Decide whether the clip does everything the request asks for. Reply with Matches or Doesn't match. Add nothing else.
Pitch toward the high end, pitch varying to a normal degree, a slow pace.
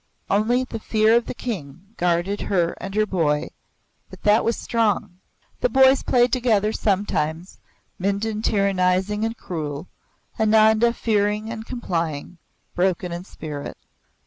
Matches